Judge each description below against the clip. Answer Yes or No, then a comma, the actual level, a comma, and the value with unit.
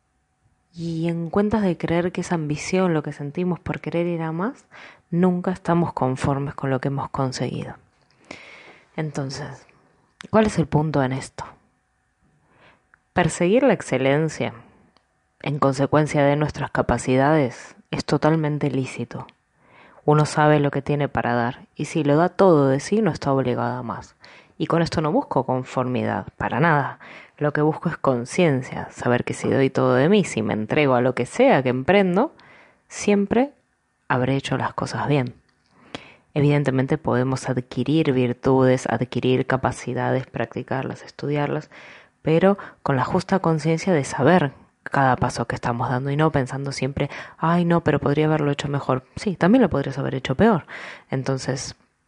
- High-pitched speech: No, medium, 145 Hz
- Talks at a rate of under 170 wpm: Yes, average, 155 wpm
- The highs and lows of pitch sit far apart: No, average, 4.2 semitones